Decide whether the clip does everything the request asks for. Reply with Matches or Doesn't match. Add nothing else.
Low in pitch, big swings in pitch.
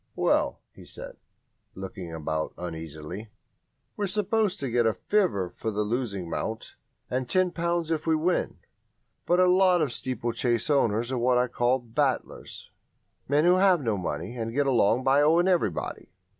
Matches